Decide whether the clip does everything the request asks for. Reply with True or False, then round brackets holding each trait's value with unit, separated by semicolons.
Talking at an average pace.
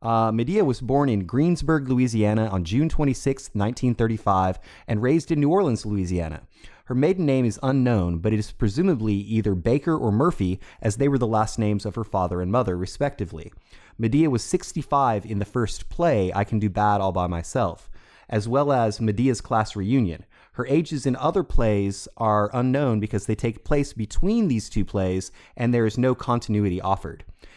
True (190 wpm)